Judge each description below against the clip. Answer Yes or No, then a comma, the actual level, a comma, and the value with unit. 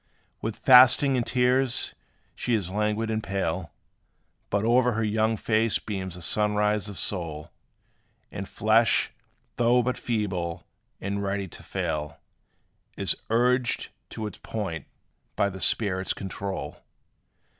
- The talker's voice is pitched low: Yes, low, 105 Hz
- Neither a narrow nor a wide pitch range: Yes, average, 3.2 semitones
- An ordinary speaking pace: No, slow, 125 wpm